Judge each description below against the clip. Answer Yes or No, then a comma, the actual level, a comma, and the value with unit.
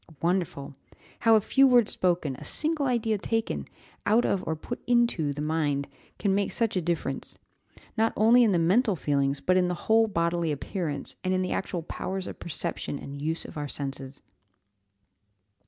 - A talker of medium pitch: Yes, medium, 180 Hz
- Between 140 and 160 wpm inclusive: No, average, 175 wpm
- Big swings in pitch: Yes, wide, 6.4 semitones